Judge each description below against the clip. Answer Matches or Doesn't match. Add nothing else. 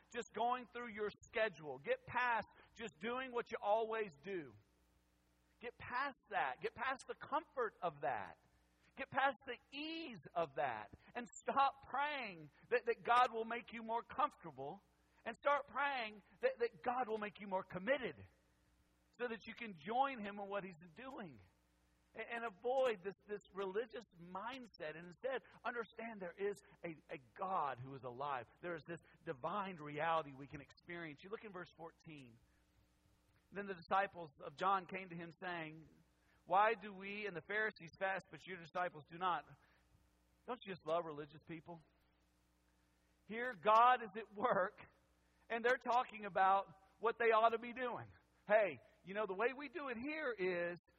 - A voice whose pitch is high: Matches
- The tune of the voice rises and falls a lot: Matches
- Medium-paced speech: Matches